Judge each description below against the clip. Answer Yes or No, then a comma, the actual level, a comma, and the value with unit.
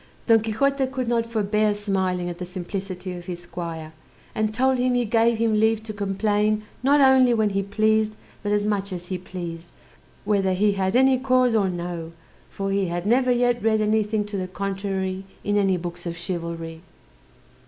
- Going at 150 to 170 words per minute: No, average, 185 wpm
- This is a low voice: No, high, 205 Hz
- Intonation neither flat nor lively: Yes, average, 3.5 semitones